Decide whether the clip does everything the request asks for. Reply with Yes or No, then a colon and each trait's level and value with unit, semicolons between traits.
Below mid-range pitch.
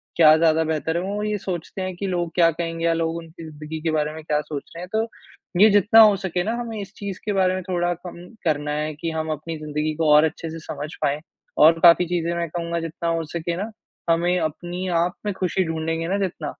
No: medium, 170 Hz